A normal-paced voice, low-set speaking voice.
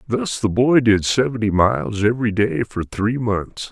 Yes: average, 180 wpm; low, 110 Hz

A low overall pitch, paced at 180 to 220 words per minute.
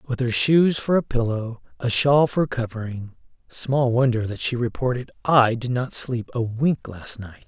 Yes: low, 120 Hz; average, 185 wpm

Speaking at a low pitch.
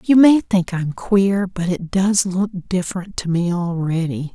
No: medium, 185 Hz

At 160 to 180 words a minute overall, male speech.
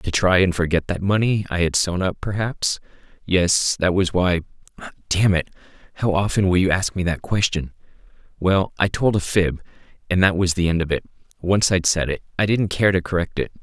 No: fast, 205 wpm; male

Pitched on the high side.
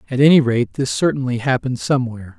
No: low, 130 Hz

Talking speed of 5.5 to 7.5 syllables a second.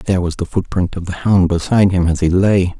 Yes: 5.8 syllables/s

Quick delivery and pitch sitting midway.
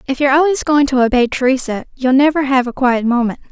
No: fast, 220 wpm; very high, 265 Hz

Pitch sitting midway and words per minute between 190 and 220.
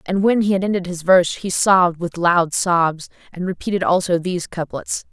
Yes: medium, 180 Hz; average, 200 wpm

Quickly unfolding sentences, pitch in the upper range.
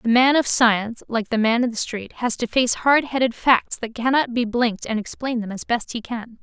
Yes: fast, 245 wpm; high, 235 Hz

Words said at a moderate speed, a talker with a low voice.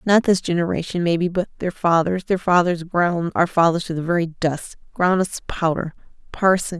No: average, 185 wpm; medium, 175 Hz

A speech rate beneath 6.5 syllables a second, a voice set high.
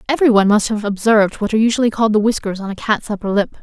No: 7.9 syllables/s; high, 215 Hz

